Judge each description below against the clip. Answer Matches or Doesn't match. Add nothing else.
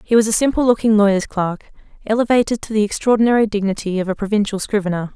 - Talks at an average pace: Matches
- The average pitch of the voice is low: Doesn't match